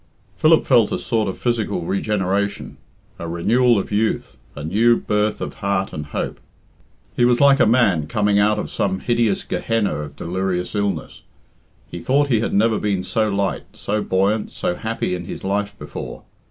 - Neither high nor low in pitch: No, low, 105 Hz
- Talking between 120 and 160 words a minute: No, average, 175 wpm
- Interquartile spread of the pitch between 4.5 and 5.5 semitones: No, average, 3.2 semitones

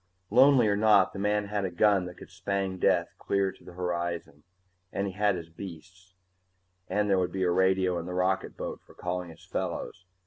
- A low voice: Yes, very low, 95 Hz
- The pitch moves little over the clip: Yes, narrow, 2.0 semitones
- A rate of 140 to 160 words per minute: No, average, 200 wpm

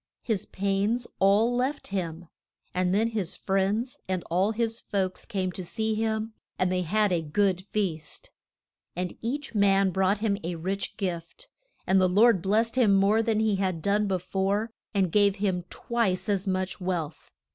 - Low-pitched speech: No, high, 195 Hz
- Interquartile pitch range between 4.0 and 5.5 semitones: No, average, 2.9 semitones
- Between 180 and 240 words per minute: No, average, 170 wpm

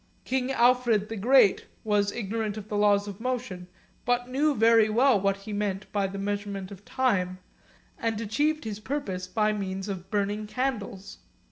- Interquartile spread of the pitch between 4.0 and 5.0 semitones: No, average, 3.3 semitones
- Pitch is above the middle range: Yes, high, 210 Hz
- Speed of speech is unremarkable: Yes, average, 165 wpm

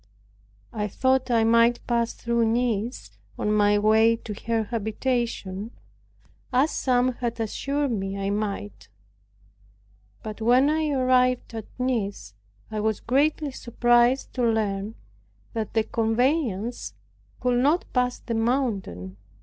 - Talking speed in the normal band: No, slow, 125 wpm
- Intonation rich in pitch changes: No, average, 2.8 semitones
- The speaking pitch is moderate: No, high, 230 Hz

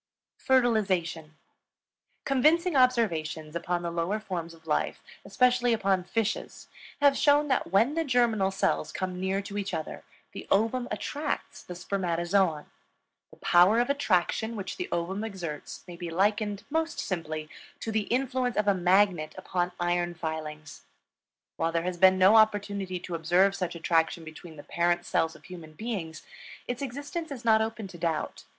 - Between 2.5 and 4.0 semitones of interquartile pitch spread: No, average, 5.0 semitones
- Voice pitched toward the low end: No, high, 190 Hz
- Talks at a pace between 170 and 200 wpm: No, average, 155 wpm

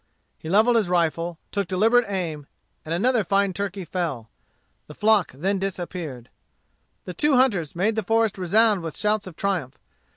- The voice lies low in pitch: No, high, 190 Hz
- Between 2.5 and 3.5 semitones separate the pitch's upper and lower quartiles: No, average, 4.2 semitones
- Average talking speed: Yes, average, 160 wpm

